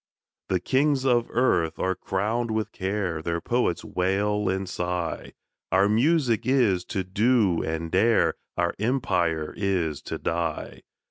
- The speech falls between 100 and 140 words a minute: Yes, slow, 135 wpm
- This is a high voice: No, very low, 95 Hz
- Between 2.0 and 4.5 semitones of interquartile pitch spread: No, average, 5.0 semitones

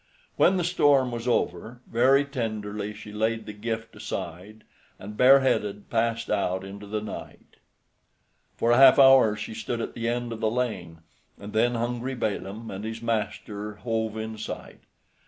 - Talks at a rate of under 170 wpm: Yes, average, 160 wpm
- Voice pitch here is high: No, low, 115 Hz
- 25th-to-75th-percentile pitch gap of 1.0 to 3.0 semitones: Yes, narrow, 2.5 semitones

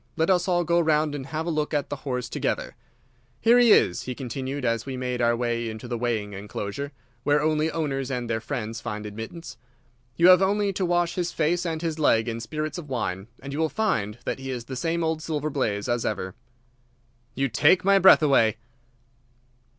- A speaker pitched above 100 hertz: Yes, medium, 140 Hz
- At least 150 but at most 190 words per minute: No, fast, 205 wpm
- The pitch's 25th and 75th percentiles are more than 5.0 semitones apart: Yes, wide, 5.6 semitones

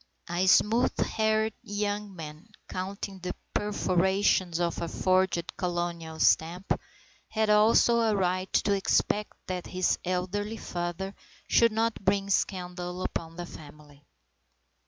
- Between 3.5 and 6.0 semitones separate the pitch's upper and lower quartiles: No, average, 2.9 semitones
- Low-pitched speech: No, medium, 185 Hz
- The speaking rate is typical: No, slow, 120 wpm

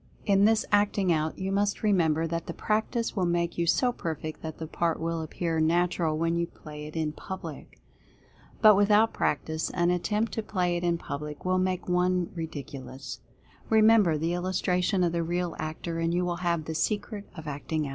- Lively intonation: No, average, 3.0 semitones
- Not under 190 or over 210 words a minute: Yes, average, 195 wpm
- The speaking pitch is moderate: Yes, medium, 175 Hz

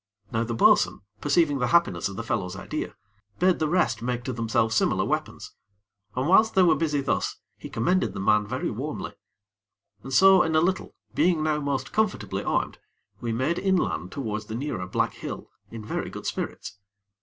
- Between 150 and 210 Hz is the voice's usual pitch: No, low, 135 Hz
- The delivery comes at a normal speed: Yes, average, 180 wpm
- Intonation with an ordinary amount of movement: No, wide, 7.2 semitones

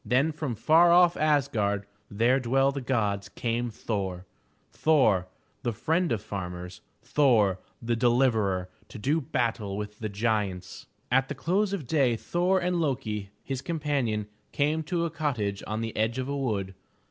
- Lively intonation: Yes, wide, 6.0 semitones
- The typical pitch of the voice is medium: No, low, 120 Hz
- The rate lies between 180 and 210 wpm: No, average, 160 wpm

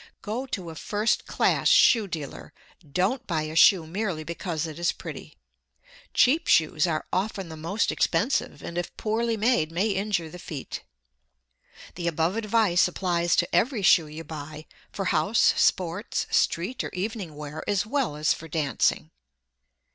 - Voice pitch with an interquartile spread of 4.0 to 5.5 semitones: Yes, average, 5.1 semitones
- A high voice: No, medium, 175 Hz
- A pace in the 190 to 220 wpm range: No, average, 155 wpm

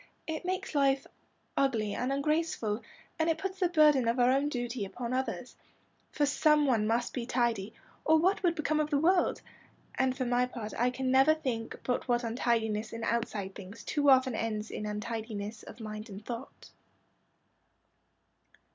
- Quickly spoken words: No, average, 170 wpm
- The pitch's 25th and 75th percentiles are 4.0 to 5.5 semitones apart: Yes, average, 4.4 semitones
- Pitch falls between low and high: No, very high, 250 Hz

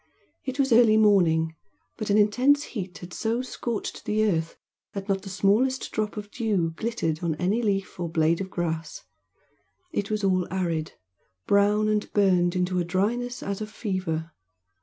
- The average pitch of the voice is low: No, high, 200 Hz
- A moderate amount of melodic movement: Yes, average, 3.6 semitones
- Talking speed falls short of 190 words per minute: Yes, average, 165 wpm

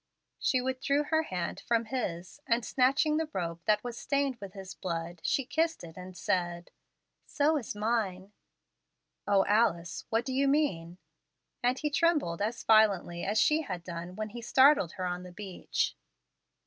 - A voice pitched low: No, high, 215 Hz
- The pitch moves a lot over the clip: Yes, wide, 6.7 semitones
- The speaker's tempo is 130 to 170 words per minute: Yes, average, 165 wpm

